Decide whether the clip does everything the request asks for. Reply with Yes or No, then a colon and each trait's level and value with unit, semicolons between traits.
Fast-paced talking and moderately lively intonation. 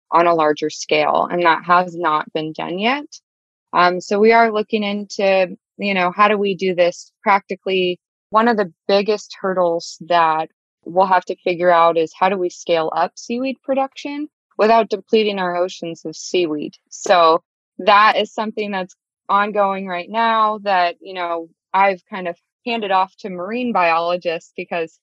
No: average, 170 wpm; average, 3.6 semitones